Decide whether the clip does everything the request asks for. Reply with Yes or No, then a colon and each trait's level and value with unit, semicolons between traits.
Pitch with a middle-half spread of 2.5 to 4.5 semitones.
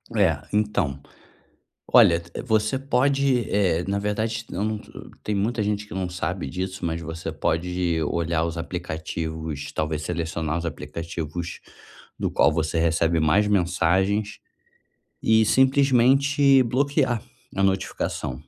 No: average, 4.9 semitones